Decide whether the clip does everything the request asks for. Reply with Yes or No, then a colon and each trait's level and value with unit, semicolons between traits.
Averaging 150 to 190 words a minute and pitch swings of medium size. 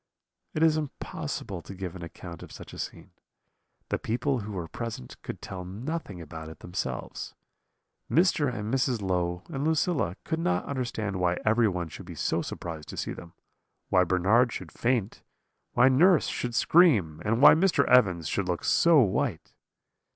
No: average, 165 wpm; wide, 7.0 semitones